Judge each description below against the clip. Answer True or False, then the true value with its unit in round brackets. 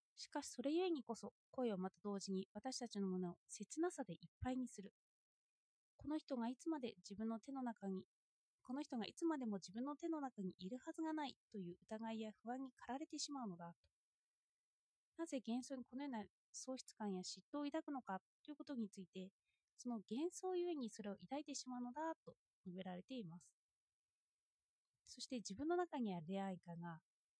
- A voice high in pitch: True (240 Hz)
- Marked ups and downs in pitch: True (6.5 semitones)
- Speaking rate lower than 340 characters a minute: False (360 characters per minute)